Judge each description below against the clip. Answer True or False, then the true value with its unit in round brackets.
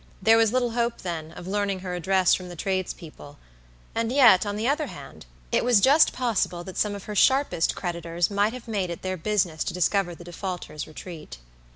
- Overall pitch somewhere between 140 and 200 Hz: True (190 Hz)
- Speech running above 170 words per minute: True (200 wpm)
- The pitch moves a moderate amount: True (4.4 semitones)